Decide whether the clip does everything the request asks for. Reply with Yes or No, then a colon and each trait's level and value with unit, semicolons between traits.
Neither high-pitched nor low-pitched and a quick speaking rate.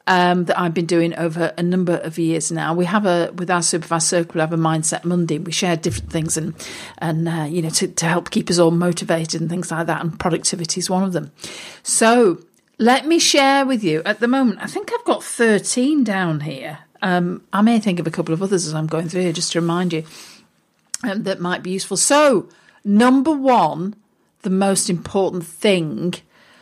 Yes: medium, 180 Hz; fast, 215 wpm